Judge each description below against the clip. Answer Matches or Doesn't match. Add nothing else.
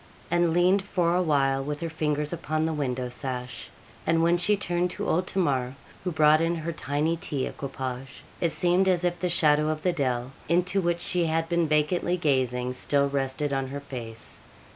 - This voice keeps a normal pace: Matches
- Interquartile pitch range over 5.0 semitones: Doesn't match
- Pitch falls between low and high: Matches